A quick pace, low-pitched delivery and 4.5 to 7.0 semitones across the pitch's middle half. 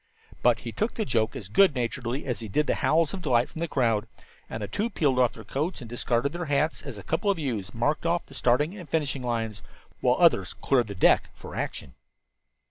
Yes: fast, 225 wpm; low, 130 Hz; wide, 5.4 semitones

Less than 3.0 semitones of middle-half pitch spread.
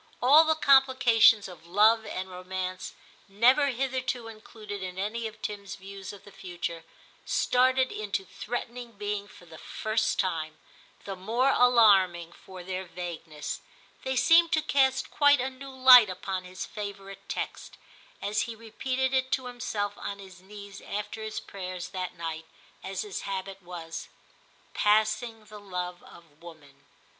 No: average, 4.8 semitones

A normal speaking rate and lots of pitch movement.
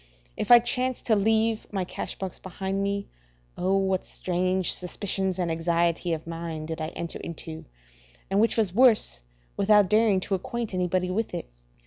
No: average, 165 wpm; average, 3.5 semitones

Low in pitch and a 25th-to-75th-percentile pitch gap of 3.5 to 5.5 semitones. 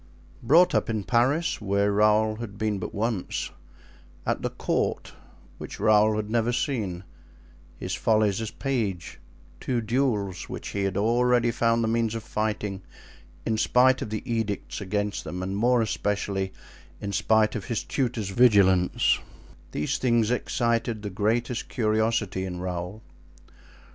No: low, 110 Hz; average, 2.7 semitones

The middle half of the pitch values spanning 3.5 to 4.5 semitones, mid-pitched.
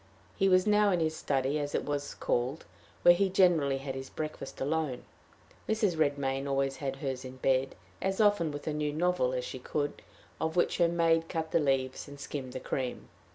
Yes: average, 3.9 semitones; medium, 145 Hz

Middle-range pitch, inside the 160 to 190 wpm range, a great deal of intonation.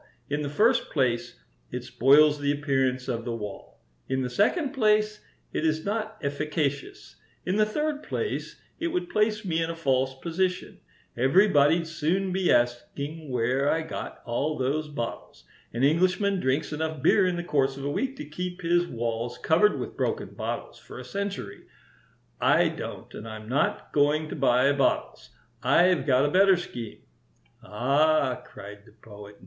Yes: medium, 150 Hz; average, 165 wpm; wide, 6.0 semitones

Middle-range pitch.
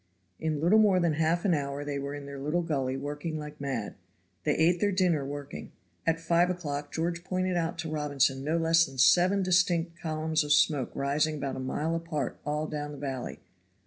Yes: medium, 155 Hz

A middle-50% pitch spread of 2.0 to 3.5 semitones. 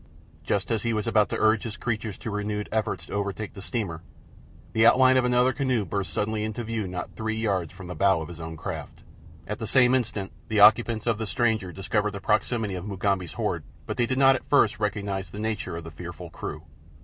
Yes: average, 2.9 semitones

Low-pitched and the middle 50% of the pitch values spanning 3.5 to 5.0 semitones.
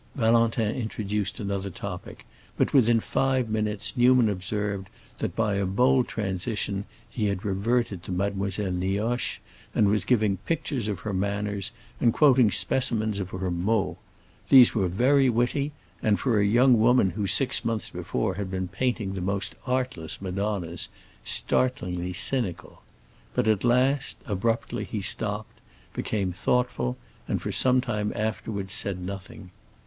Yes: low, 105 Hz; average, 3.8 semitones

